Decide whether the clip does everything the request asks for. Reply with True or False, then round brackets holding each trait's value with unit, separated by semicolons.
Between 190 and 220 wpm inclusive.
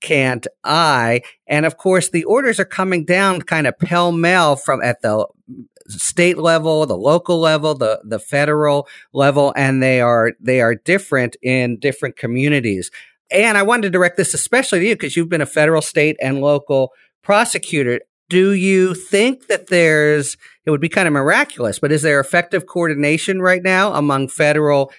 False (175 wpm)